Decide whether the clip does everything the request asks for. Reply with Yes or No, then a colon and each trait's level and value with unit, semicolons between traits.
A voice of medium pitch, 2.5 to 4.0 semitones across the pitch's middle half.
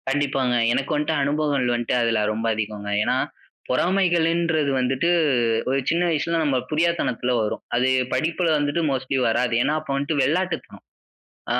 No: medium, 145 Hz; average, 4.4 semitones